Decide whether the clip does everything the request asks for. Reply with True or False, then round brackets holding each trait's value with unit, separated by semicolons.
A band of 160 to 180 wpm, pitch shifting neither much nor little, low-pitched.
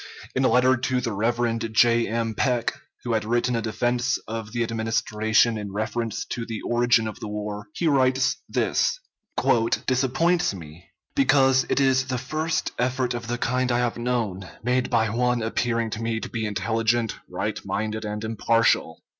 False (170 wpm; 2.3 semitones; 120 Hz)